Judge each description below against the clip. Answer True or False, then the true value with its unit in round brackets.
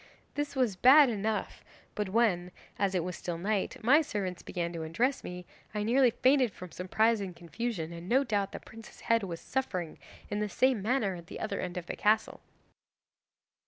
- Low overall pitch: False (205 Hz)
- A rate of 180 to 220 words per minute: True (190 wpm)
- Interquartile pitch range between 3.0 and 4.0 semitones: False (5.0 semitones)